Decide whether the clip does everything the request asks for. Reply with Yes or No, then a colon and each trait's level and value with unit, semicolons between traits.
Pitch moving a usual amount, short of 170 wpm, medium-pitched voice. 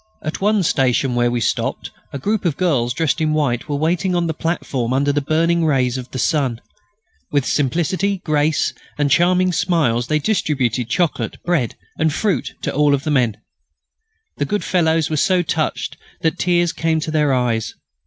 No: average, 4.5 semitones; average, 175 wpm; medium, 155 Hz